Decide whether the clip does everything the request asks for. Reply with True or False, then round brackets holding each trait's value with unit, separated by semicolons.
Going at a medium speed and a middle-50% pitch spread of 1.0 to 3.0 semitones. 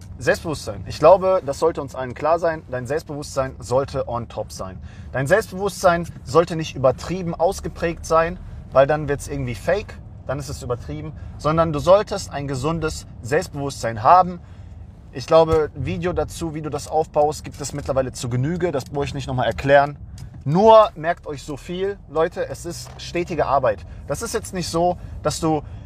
False (175 wpm; 4.3 semitones)